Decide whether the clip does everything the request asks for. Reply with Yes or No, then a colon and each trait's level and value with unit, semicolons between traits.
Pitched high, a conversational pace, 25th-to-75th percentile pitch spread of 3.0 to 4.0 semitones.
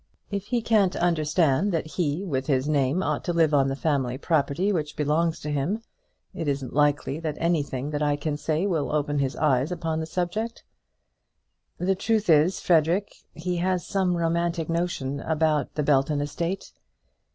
No: medium, 160 Hz; average, 170 wpm; average, 3.4 semitones